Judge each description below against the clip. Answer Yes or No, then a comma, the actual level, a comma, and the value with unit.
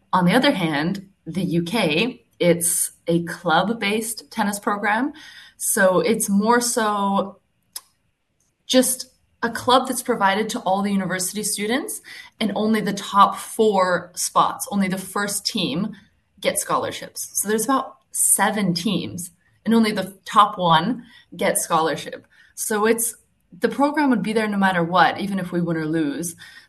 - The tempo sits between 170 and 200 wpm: No, average, 145 wpm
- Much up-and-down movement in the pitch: No, average, 4.1 semitones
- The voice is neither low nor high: No, high, 205 Hz